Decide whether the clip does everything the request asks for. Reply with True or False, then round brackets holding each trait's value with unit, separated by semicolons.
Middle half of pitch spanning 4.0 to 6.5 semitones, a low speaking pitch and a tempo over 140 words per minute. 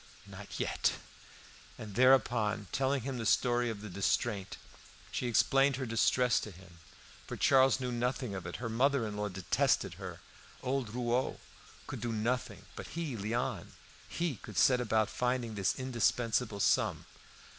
False (3.3 semitones; 120 Hz; 155 wpm)